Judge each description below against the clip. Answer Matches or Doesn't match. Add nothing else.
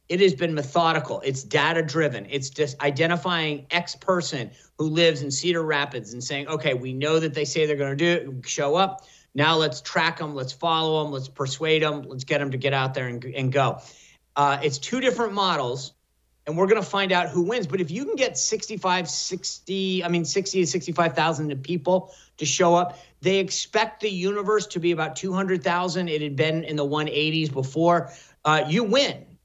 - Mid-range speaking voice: Matches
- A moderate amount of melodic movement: Matches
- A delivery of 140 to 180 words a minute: Doesn't match